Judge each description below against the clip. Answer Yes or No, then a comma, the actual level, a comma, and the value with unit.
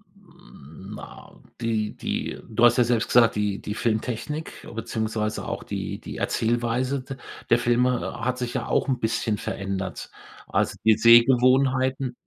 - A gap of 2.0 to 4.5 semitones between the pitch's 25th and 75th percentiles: Yes, narrow, 2.6 semitones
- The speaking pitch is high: No, low, 120 Hz